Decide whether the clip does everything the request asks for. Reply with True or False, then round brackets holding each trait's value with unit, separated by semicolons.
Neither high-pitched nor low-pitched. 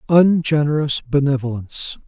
True (145 Hz)